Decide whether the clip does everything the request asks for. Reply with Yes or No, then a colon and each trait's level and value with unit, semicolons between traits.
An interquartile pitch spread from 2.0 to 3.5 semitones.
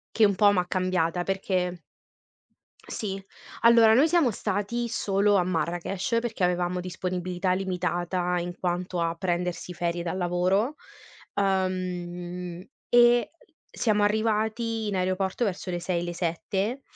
Yes: average, 2.7 semitones